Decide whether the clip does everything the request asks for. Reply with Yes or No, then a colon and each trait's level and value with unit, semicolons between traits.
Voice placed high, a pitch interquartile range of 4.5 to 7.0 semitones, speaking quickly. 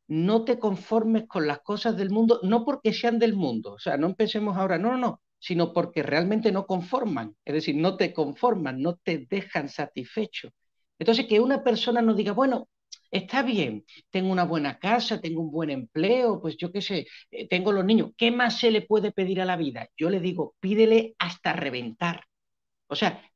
Yes: high, 195 Hz; average, 5.0 semitones; fast, 195 wpm